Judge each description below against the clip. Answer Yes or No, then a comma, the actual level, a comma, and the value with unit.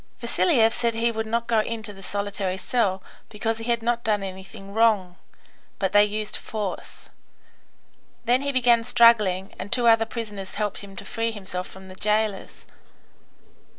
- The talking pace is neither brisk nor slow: Yes, average, 160 wpm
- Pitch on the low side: No, high, 215 Hz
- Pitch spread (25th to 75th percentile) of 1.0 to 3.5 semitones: Yes, average, 2.9 semitones